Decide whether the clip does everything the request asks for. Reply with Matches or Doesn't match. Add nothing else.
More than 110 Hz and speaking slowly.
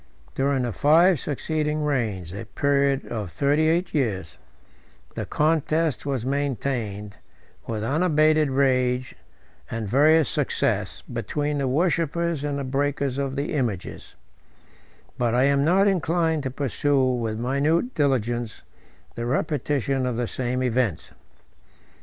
Matches